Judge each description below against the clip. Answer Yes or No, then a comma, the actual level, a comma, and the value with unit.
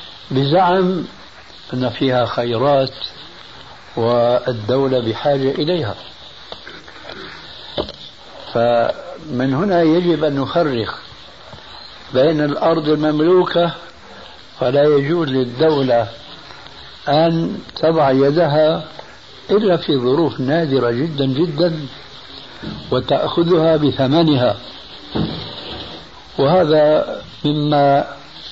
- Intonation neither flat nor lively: Yes, average, 4.2 semitones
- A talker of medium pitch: Yes, medium, 145 Hz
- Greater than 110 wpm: No, slow, 65 wpm